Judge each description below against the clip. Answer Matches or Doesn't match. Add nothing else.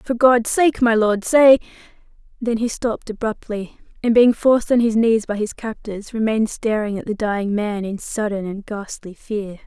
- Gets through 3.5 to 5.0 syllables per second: Matches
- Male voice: Doesn't match